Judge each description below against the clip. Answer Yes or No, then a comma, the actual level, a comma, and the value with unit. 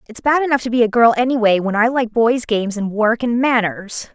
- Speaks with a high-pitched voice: Yes, high, 230 Hz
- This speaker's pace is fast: Yes, fast, 245 wpm